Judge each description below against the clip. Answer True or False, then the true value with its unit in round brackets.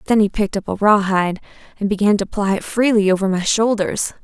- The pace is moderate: False (215 wpm)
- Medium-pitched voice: False (205 Hz)